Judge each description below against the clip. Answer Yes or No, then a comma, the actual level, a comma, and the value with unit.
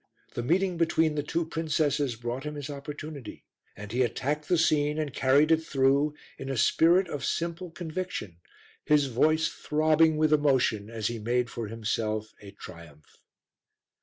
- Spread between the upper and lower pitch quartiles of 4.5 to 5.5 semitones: Yes, average, 4.8 semitones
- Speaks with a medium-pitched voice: Yes, medium, 145 Hz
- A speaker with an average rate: Yes, average, 160 wpm